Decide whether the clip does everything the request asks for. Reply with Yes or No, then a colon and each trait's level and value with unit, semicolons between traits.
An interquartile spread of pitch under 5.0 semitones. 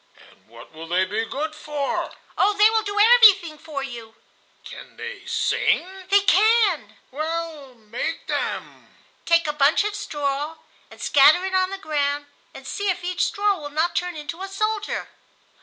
No: wide, 5.6 semitones